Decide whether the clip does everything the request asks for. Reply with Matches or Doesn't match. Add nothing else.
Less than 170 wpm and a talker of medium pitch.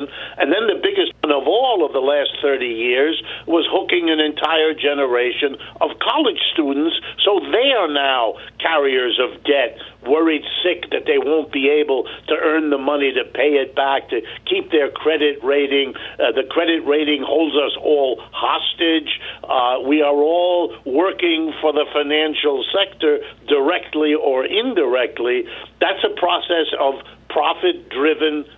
Matches